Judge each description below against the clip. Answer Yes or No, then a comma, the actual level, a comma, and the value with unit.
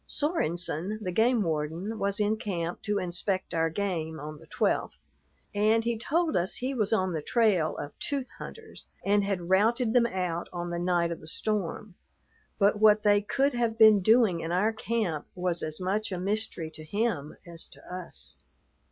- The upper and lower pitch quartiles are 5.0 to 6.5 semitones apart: No, average, 4.3 semitones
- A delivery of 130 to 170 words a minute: No, average, 180 wpm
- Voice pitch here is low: No, high, 195 Hz